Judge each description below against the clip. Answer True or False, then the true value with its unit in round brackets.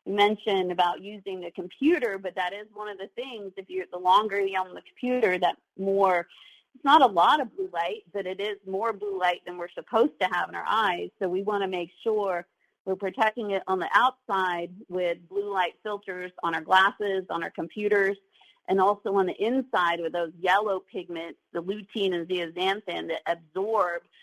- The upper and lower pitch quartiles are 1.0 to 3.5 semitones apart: True (2.4 semitones)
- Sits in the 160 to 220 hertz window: True (190 Hz)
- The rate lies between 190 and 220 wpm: True (200 wpm)